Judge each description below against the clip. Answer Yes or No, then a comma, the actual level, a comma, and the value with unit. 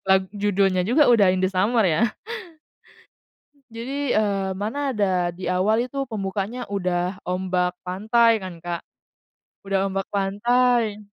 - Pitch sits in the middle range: No, high, 200 Hz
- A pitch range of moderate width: Yes, average, 3.6 semitones